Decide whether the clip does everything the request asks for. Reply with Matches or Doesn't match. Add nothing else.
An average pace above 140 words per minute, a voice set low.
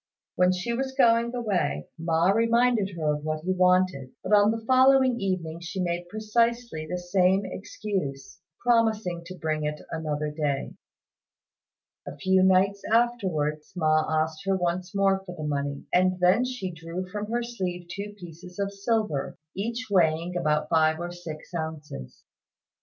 Doesn't match